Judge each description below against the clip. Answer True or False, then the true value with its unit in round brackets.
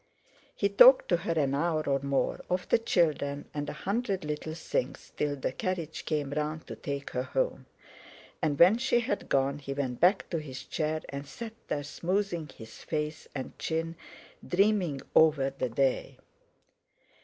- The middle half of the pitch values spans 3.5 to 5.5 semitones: True (4.2 semitones)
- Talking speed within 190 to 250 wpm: False (165 wpm)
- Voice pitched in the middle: True (155 Hz)